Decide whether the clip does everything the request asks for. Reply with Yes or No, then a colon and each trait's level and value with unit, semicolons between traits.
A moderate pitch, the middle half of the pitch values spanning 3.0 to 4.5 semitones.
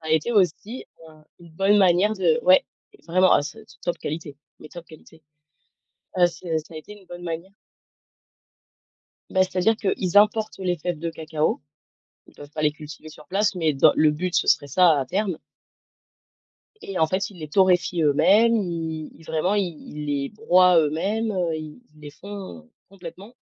Yes: medium, 175 Hz; average, 3.6 semitones